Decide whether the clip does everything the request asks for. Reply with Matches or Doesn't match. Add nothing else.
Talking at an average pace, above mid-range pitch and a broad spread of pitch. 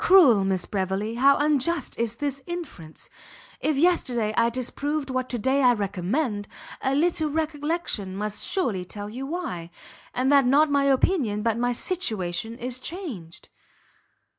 Matches